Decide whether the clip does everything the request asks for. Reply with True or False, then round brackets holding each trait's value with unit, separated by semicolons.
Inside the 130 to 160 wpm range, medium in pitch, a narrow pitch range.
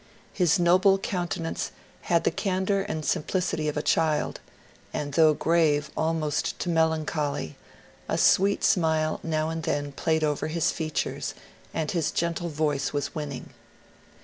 True (150 wpm; 160 Hz; 2.2 semitones)